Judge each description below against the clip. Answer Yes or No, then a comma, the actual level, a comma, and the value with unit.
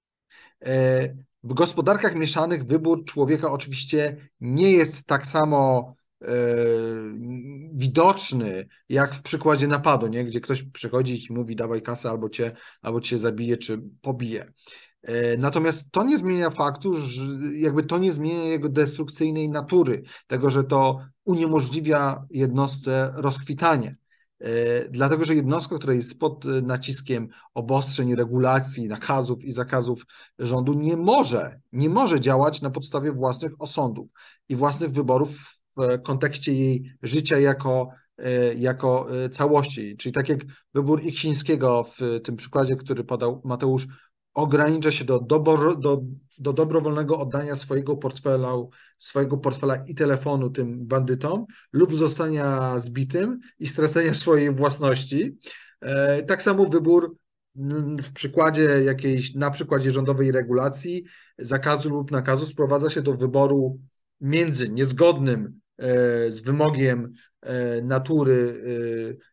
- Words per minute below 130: Yes, average, 120 wpm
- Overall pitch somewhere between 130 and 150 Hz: Yes, medium, 140 Hz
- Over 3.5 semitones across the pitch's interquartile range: No, average, 3.2 semitones